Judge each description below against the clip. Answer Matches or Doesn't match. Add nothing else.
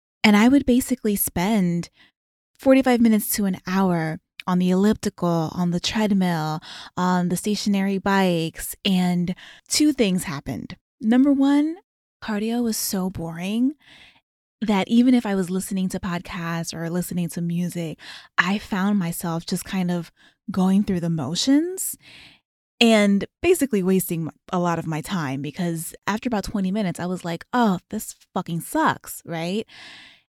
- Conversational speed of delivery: Matches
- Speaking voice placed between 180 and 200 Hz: Matches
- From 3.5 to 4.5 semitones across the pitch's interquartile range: Matches